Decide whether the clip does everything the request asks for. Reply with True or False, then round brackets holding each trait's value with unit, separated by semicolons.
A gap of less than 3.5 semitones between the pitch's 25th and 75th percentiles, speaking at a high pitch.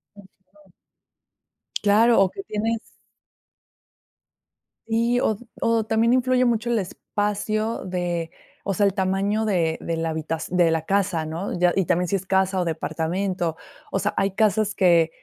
False (3.8 semitones; 195 Hz)